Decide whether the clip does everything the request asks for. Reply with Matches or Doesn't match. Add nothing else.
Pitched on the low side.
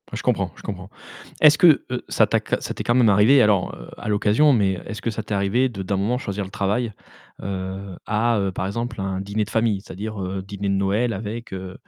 Matches